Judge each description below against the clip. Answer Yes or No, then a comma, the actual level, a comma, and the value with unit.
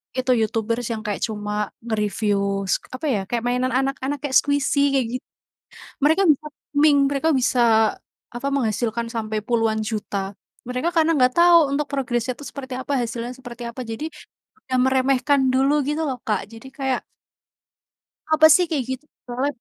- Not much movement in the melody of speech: No, average, 3.6 semitones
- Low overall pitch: No, very high, 255 Hz